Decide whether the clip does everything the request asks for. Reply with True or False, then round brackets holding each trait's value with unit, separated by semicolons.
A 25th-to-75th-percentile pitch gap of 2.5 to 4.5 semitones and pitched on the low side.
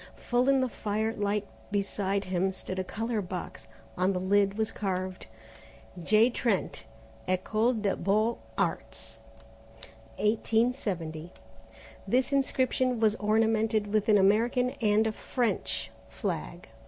False (3.0 semitones; 210 Hz)